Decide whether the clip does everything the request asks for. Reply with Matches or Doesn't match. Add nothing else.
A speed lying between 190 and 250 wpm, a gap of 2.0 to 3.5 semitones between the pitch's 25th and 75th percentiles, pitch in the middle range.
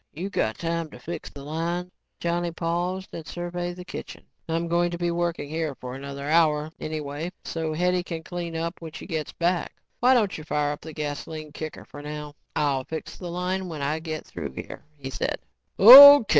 Matches